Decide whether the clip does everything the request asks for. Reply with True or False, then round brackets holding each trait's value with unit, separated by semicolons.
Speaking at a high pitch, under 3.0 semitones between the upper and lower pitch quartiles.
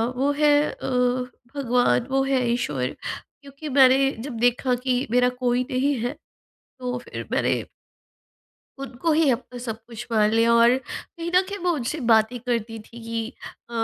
True (250 Hz; 2.5 semitones)